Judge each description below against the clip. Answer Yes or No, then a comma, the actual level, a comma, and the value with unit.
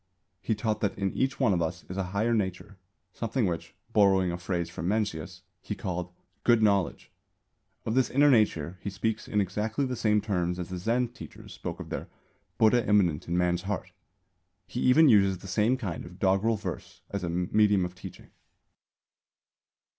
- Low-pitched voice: Yes, low, 100 Hz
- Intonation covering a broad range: No, average, 3.7 semitones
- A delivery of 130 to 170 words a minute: No, average, 180 wpm